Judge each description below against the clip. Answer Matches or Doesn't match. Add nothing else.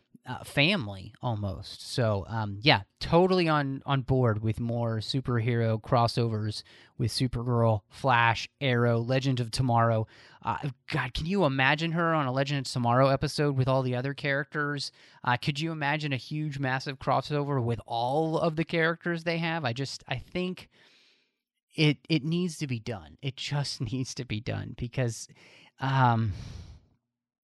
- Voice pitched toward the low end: Matches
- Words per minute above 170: Doesn't match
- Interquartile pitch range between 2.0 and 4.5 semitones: Matches